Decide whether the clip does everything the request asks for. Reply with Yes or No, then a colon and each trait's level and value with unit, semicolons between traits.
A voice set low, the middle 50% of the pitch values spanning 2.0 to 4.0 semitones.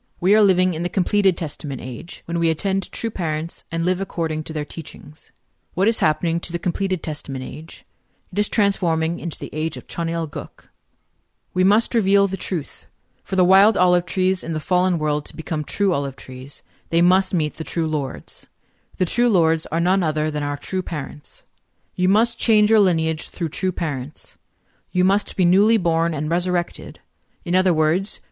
No: medium, 170 Hz; average, 3.4 semitones